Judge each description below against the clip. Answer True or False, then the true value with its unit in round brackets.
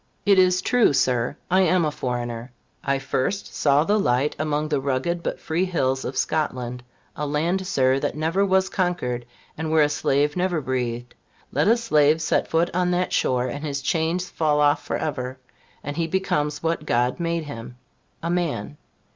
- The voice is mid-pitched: True (150 Hz)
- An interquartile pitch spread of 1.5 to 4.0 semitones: False (4.9 semitones)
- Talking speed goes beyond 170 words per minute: True (180 wpm)